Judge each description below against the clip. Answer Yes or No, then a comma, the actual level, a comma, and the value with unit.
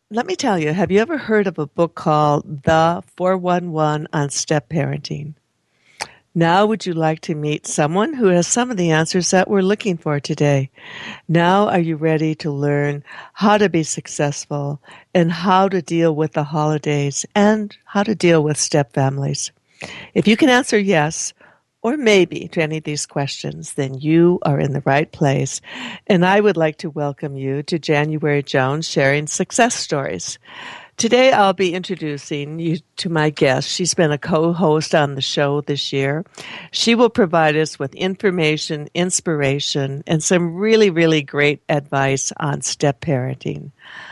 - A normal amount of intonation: Yes, average, 4.2 semitones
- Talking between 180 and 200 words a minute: No, average, 170 wpm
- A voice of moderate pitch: Yes, medium, 160 Hz